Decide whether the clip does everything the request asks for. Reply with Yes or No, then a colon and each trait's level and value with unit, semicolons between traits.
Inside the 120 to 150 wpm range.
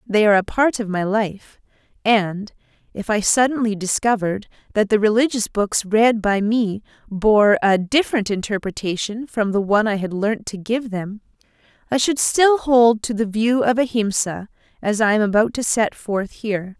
No: average, 175 wpm